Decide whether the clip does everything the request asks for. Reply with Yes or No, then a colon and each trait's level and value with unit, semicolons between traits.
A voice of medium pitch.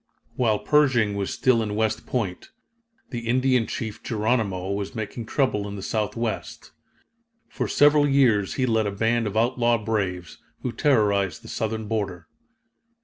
No: low, 110 Hz